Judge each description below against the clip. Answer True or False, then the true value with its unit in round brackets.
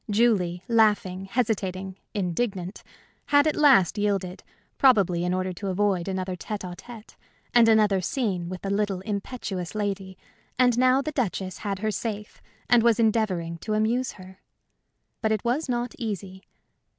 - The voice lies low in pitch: False (205 Hz)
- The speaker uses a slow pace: False (150 wpm)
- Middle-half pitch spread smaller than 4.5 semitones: True (3.7 semitones)